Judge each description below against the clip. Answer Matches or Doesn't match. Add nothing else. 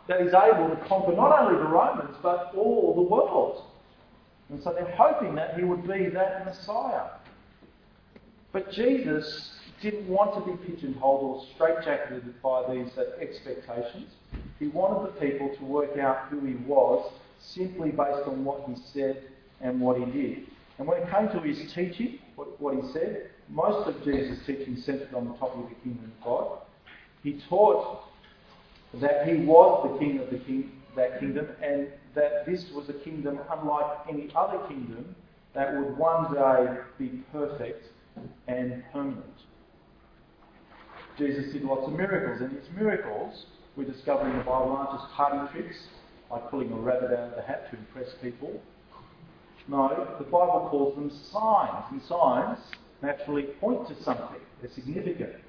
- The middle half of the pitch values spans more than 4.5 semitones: Matches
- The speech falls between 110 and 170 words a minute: Matches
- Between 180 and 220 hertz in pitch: Doesn't match